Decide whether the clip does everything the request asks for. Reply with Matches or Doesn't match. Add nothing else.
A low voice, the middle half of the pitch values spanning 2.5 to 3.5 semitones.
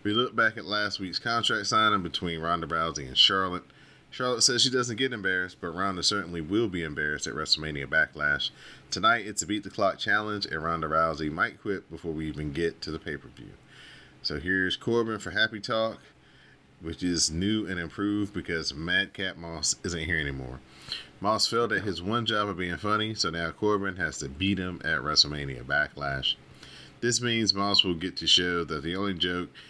Doesn't match